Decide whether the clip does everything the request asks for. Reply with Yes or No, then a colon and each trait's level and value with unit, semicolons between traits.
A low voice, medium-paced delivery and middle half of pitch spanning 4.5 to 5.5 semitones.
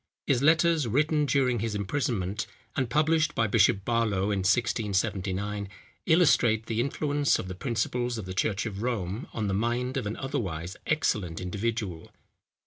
Yes: low, 115 Hz; average, 150 wpm; average, 4.9 semitones